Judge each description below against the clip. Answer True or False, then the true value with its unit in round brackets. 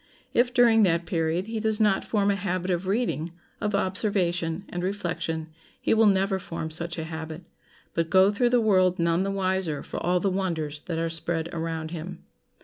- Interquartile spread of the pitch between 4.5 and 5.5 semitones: False (3.2 semitones)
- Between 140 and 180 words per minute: False (190 wpm)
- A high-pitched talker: False (180 Hz)